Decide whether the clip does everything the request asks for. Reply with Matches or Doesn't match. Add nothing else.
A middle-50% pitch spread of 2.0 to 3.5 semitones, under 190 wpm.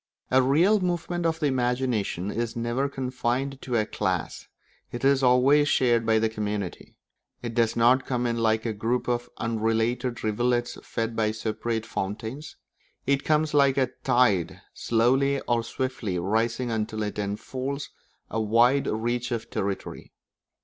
Matches